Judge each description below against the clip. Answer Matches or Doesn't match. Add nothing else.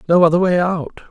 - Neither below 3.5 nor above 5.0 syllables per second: Doesn't match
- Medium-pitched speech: Matches